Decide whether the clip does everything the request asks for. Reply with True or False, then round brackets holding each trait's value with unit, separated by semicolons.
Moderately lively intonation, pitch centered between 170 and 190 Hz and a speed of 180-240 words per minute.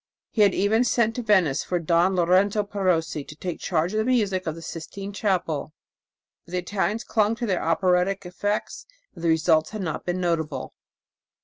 True (3.6 semitones; 185 Hz; 185 wpm)